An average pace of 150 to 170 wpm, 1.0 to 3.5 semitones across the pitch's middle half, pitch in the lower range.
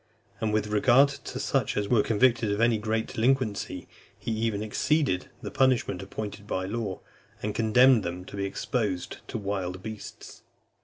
Yes: average, 160 wpm; average, 2.7 semitones; low, 110 Hz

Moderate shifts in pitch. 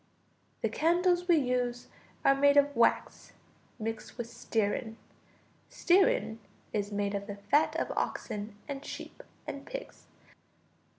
No: wide, 5.7 semitones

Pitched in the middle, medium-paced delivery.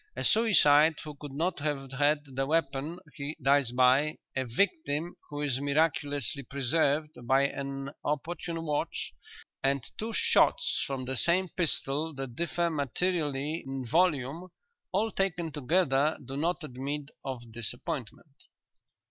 No: medium, 145 Hz; slow, 130 wpm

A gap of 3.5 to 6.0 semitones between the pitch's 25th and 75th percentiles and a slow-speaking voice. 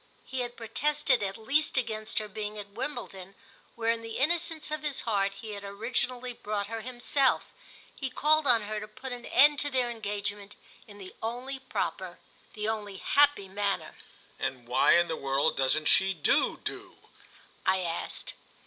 No: average, 4.3 semitones; average, 170 wpm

